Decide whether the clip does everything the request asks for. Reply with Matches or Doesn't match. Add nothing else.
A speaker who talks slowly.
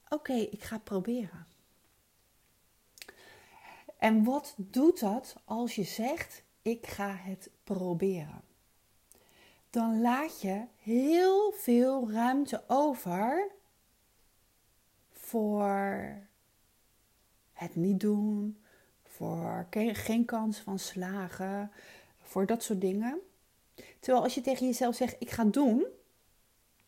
Matches